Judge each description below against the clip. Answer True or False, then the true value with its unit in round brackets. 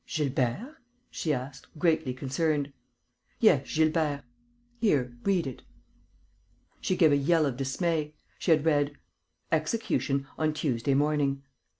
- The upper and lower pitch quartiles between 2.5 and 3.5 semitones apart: True (2.8 semitones)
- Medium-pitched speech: True (150 Hz)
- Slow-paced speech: True (115 wpm)